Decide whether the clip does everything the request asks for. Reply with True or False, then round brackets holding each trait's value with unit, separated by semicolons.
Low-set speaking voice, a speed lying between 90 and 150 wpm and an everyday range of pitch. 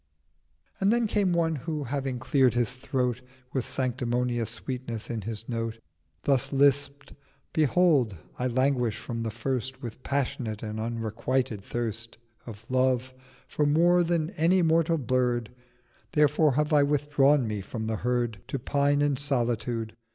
True (130 Hz; 145 wpm; 3.7 semitones)